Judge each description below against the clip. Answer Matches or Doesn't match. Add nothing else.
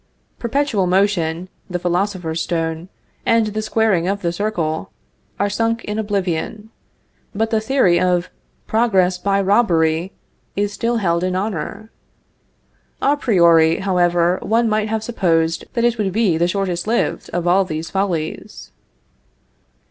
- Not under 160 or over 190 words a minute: Doesn't match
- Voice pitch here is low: Doesn't match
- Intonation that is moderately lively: Matches